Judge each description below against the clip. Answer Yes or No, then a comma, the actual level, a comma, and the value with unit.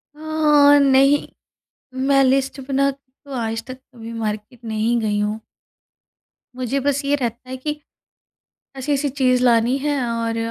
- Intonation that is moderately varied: Yes, average, 3.3 semitones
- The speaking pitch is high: Yes, very high, 255 Hz